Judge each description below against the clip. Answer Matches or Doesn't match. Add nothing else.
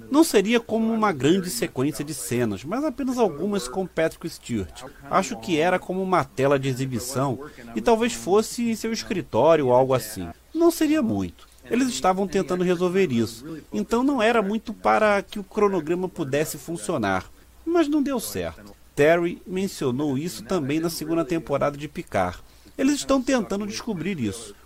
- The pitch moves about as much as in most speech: Doesn't match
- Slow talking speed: Doesn't match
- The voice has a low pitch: Doesn't match